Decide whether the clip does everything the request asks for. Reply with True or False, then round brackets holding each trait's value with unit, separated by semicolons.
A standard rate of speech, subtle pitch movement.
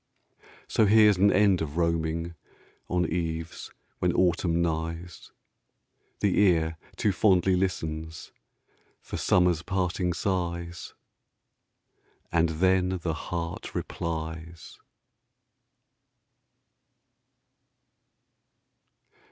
False (80 wpm; 2.1 semitones)